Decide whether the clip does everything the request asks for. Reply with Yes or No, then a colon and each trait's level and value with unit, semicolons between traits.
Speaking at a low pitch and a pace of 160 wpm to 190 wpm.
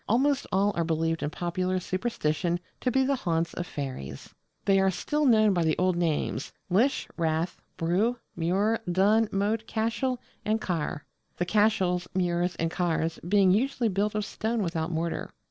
No: medium, 185 Hz; average, 165 wpm